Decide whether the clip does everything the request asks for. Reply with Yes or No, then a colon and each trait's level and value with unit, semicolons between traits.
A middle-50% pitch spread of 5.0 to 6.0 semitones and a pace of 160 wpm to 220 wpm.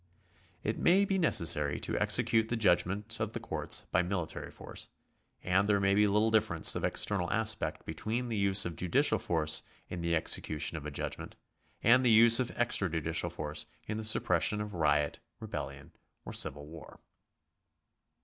Yes: wide, 5.5 semitones; average, 165 wpm